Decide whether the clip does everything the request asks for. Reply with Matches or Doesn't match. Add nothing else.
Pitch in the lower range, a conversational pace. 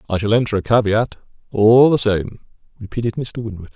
Matches